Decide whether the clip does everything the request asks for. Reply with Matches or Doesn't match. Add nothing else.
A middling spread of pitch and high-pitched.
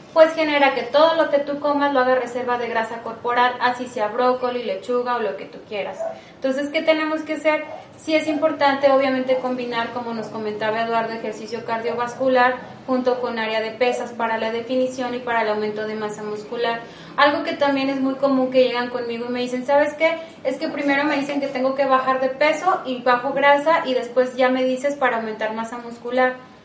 Matches